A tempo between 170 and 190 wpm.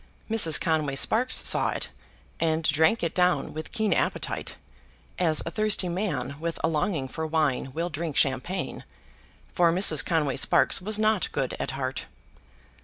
No: average, 155 wpm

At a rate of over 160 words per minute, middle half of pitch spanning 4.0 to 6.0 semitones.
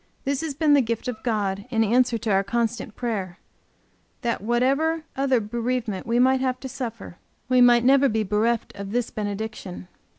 No: average, 175 wpm; average, 3.0 semitones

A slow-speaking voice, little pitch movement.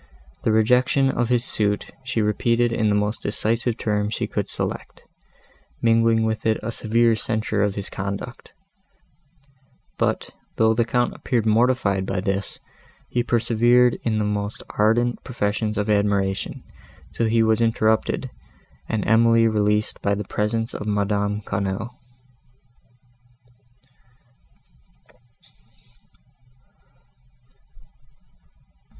Yes: slow, 110 wpm; narrow, 2.1 semitones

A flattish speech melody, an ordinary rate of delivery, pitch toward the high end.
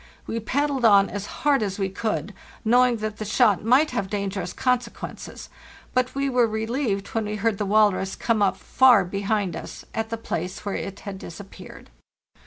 No: average, 3.4 semitones; average, 180 wpm; high, 215 Hz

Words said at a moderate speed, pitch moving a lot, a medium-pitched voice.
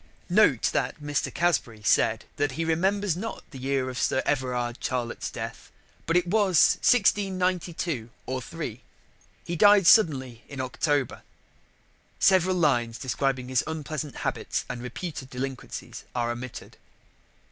No: slow, 130 wpm; wide, 5.7 semitones; medium, 145 Hz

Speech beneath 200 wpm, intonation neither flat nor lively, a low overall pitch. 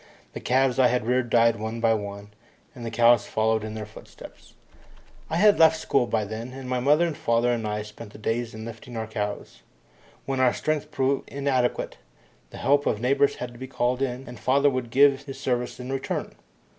No: fast, 205 wpm; average, 3.2 semitones; low, 125 Hz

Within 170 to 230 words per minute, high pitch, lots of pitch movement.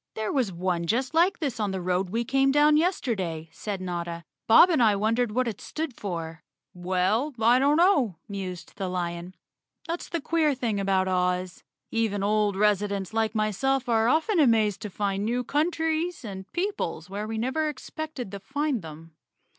Yes: average, 175 wpm; high, 215 Hz; wide, 6.4 semitones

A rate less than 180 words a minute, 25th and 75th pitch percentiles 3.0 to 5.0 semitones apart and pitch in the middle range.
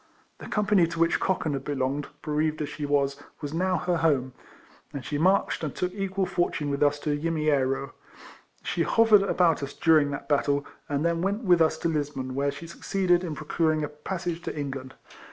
No: average, 200 wpm; average, 3.6 semitones; medium, 155 Hz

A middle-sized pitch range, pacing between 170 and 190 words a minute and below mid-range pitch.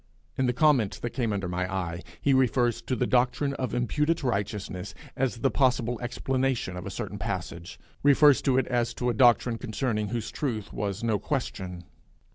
Yes: average, 4.1 semitones; average, 180 wpm; low, 120 Hz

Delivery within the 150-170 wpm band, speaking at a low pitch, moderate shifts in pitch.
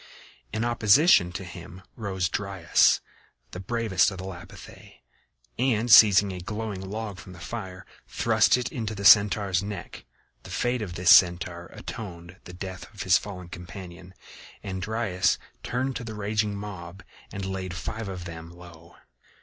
Yes: average, 155 wpm; very low, 95 Hz; average, 3.2 semitones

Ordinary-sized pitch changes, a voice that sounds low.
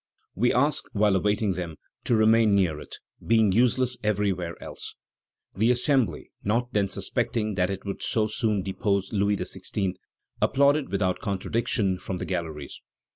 Yes: average, 3.3 semitones; low, 105 Hz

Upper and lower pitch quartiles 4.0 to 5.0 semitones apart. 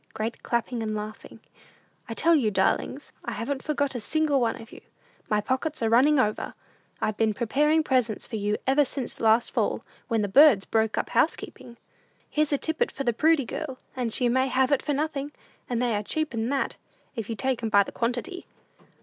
Yes: average, 4.3 semitones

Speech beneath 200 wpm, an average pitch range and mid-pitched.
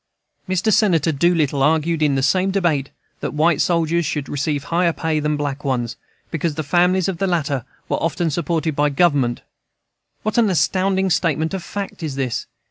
Yes: average, 175 wpm; average, 3.5 semitones; medium, 160 Hz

